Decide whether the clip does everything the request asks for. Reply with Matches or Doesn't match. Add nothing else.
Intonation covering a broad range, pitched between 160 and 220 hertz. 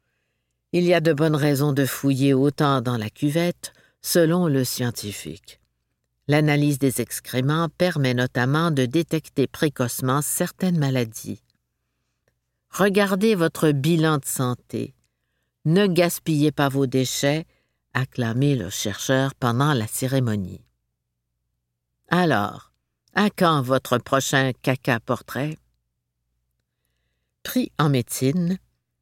Doesn't match